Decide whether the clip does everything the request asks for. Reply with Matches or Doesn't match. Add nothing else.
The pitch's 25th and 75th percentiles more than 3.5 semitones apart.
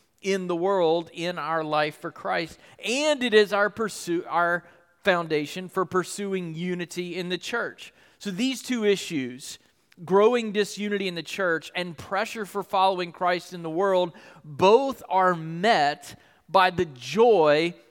Doesn't match